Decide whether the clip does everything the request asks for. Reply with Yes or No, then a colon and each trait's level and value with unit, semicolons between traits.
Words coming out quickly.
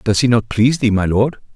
Yes: fast, 270 wpm